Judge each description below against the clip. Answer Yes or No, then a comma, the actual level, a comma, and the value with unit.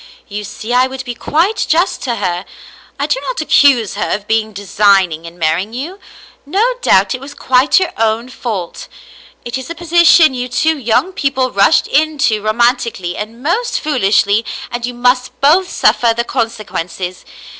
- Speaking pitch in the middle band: No, high, 245 Hz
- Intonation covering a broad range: Yes, wide, 5.9 semitones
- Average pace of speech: Yes, average, 170 wpm